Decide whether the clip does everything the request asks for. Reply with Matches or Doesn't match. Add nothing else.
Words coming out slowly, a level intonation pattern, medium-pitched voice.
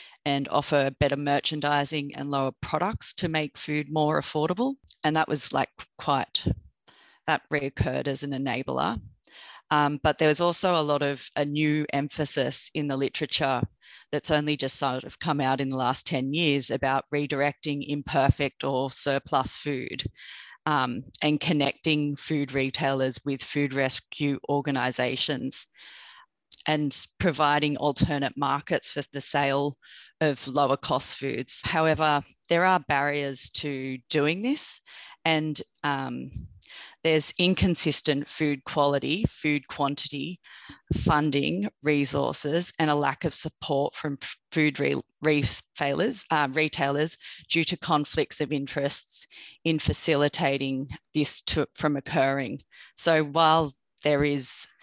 Matches